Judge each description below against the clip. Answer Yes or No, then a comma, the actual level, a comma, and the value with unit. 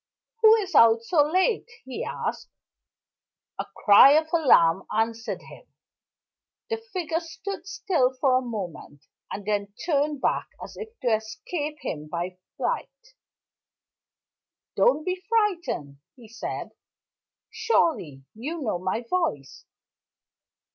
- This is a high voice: Yes, very high, 270 Hz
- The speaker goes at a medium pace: No, slow, 120 wpm